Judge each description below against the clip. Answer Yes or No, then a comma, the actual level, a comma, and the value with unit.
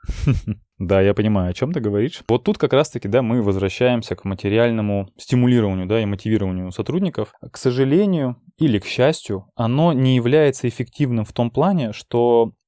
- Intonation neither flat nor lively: Yes, average, 4.3 semitones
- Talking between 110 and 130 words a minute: No, fast, 160 wpm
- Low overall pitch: Yes, low, 120 Hz